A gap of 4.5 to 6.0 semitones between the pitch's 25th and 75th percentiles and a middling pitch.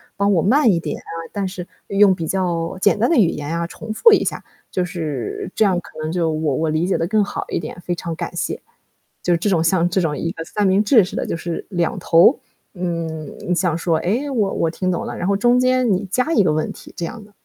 No: average, 3.6 semitones; medium, 180 Hz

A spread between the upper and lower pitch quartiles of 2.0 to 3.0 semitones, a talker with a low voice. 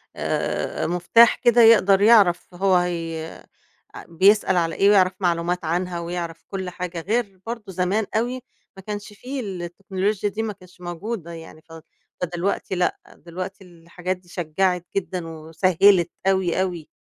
No: narrow, 2.6 semitones; medium, 185 Hz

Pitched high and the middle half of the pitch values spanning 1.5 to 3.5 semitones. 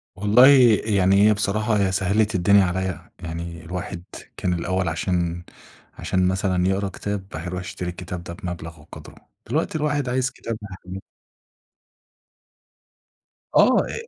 No: very low, 95 Hz; average, 2.8 semitones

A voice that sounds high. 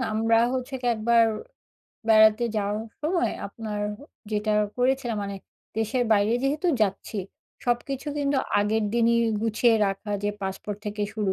Yes: high, 220 Hz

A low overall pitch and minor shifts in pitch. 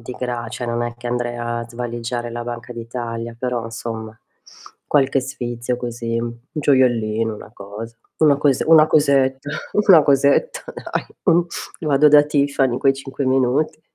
No: low, 125 Hz; average, 3.0 semitones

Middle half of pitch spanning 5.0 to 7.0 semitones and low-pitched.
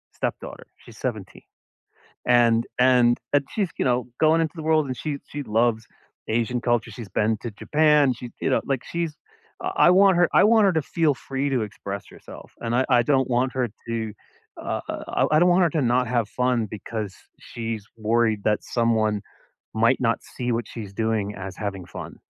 No: average, 4.3 semitones; low, 120 Hz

